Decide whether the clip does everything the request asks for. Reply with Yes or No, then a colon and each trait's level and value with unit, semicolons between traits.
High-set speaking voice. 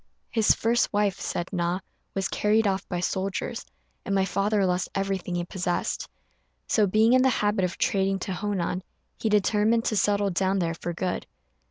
Yes: high, 195 Hz